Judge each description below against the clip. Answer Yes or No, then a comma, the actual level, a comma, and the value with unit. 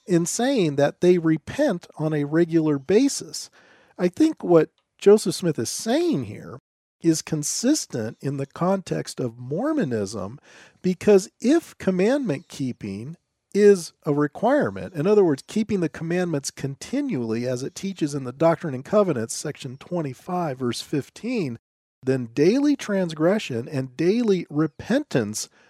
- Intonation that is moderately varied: No, wide, 6.6 semitones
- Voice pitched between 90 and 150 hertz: No, medium, 165 Hz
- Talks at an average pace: No, slow, 130 wpm